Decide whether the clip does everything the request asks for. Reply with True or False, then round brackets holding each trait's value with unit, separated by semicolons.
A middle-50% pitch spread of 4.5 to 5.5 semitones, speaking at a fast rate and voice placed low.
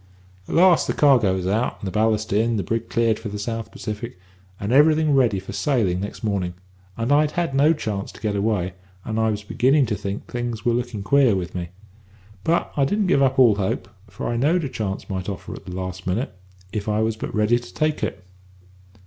True (4.9 semitones; 220 wpm; 110 Hz)